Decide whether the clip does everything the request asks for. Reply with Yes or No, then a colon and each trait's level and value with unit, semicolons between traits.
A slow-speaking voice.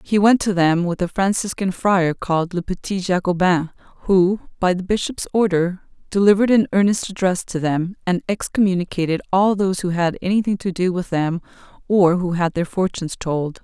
No: average, 175 wpm